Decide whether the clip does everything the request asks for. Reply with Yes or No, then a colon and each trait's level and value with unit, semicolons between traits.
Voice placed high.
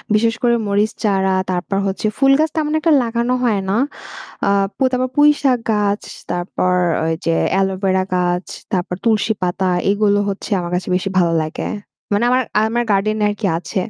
Yes: high, 205 Hz